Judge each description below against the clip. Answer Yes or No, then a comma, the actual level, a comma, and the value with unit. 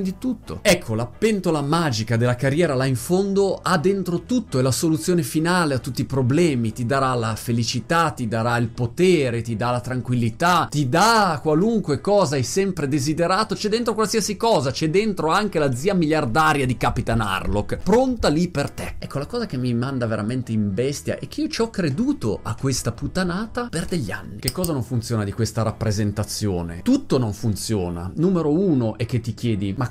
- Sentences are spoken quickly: Yes, fast, 195 wpm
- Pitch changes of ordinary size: No, wide, 7.3 semitones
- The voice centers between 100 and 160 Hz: Yes, medium, 140 Hz